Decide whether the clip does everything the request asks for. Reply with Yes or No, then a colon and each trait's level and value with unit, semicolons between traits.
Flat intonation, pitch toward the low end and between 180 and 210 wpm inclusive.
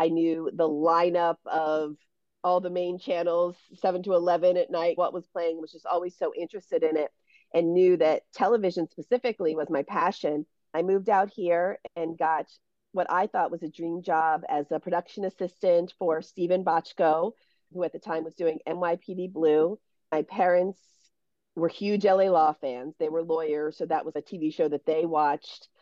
No: narrow, 2.2 semitones; medium, 170 Hz; average, 185 wpm